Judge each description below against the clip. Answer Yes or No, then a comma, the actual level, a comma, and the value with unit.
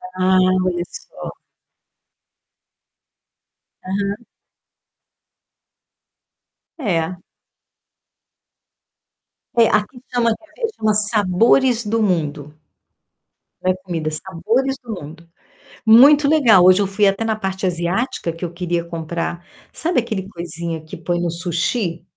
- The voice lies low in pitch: No, high, 190 Hz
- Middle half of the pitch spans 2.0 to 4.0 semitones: No, average, 4.7 semitones